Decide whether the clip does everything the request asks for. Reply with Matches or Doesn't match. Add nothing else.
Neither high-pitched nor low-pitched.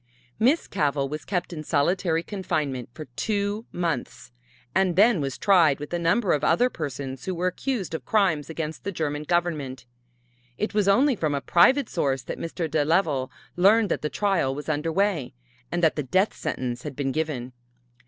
Matches